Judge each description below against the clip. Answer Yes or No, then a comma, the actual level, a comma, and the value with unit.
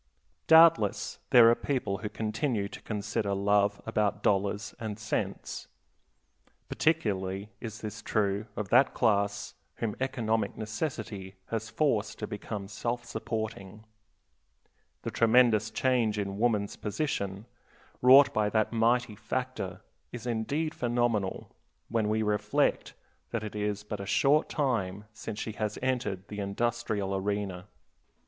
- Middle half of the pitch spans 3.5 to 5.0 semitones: No, average, 2.7 semitones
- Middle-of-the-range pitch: No, low, 110 Hz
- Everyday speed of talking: No, slow, 125 wpm